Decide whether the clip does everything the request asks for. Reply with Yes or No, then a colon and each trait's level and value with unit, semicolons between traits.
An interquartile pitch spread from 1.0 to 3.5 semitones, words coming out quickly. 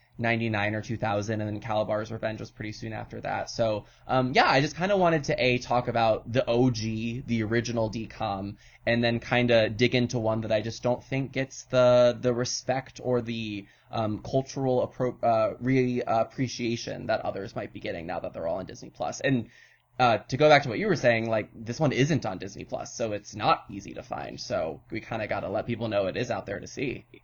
Yes: narrow, 2.4 semitones; fast, 225 wpm